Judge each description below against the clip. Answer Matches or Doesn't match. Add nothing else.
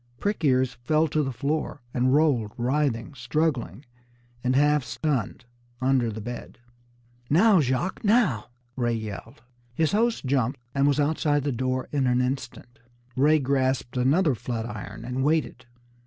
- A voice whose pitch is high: Doesn't match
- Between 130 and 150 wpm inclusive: Matches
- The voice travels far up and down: Doesn't match